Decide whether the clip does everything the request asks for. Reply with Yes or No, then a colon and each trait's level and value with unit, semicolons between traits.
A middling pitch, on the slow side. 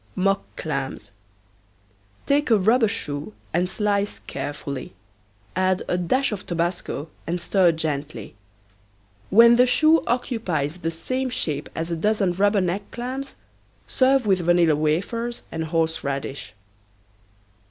Yes: medium, 180 Hz; slow, 120 wpm